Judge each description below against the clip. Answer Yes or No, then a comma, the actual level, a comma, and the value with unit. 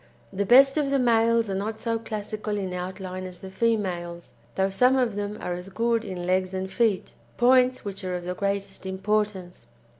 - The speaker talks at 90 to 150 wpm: No, average, 190 wpm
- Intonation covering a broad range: No, average, 3.6 semitones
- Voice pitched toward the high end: Yes, high, 200 Hz